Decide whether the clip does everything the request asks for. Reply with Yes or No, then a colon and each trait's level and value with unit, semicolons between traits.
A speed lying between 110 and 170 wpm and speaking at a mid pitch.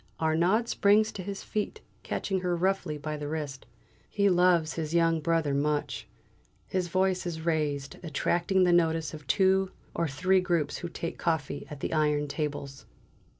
Yes: average, 160 wpm; medium, 165 Hz